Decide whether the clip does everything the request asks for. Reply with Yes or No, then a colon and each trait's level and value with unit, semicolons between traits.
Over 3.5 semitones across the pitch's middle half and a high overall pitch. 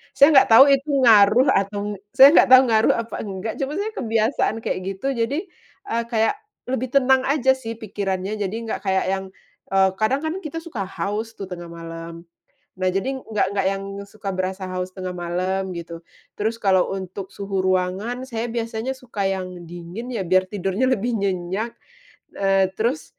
Yes: average, 4.0 semitones; high, 205 Hz